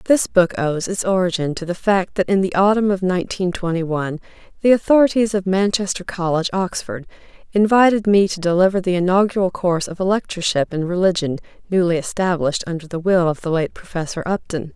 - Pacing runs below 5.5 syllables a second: No, 6.0 syllables/s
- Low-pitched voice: No, medium, 185 Hz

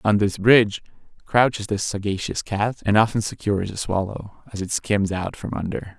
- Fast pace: No, average, 180 wpm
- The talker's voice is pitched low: Yes, low, 105 Hz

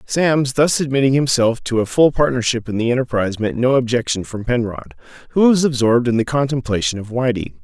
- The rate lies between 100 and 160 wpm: No, average, 190 wpm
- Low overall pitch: Yes, low, 125 Hz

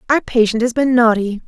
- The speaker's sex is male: No, female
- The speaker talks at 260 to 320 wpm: No, fast, 205 wpm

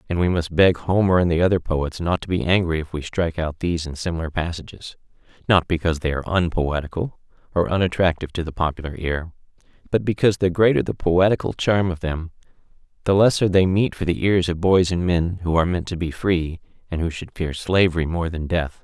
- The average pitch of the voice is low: Yes, very low, 85 Hz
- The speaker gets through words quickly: Yes, fast, 215 wpm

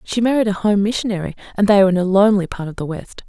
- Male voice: No, female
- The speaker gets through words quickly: Yes, fast, 275 wpm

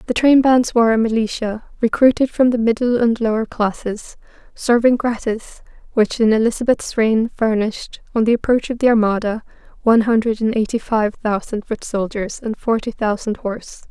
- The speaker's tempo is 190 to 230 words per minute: No, average, 160 wpm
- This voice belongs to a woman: Yes, female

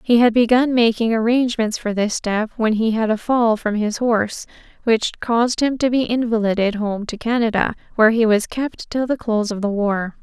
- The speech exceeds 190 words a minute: Yes, fast, 205 wpm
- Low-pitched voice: No, high, 225 Hz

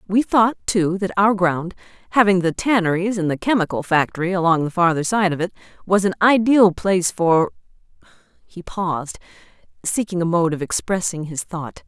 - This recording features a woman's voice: Yes, female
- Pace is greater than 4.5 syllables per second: Yes, 5.2 syllables/s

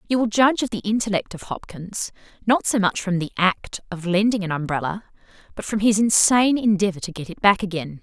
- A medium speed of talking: No, fast, 210 wpm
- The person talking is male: No, female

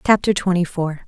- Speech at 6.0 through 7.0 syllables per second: No, 5.6 syllables/s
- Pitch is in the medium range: Yes, medium, 180 Hz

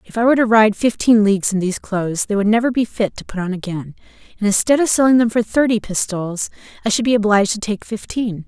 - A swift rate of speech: Yes, fast, 240 wpm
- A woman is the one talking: Yes, female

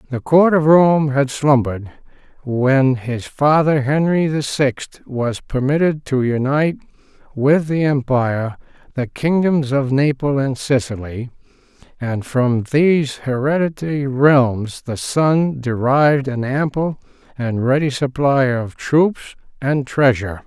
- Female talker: No, male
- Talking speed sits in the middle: No, slow, 125 wpm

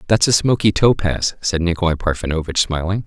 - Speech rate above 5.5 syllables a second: Yes, 5.8 syllables/s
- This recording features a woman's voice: No, male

